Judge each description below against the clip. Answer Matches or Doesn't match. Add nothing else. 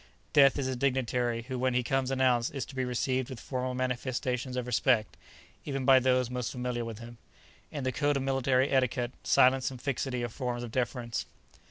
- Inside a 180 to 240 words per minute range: Matches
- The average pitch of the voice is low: Matches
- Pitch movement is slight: Matches